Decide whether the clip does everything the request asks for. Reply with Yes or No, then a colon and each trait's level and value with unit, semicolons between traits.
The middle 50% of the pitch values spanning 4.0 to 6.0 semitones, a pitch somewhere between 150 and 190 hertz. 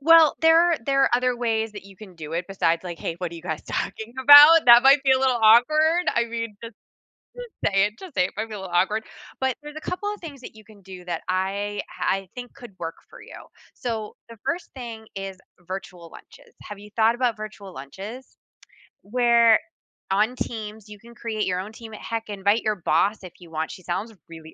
No: average, 4.5 semitones; high, 220 Hz